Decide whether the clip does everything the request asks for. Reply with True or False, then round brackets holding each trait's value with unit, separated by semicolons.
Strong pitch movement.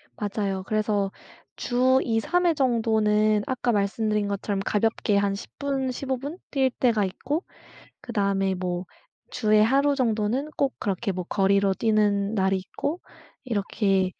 False (4.3 semitones)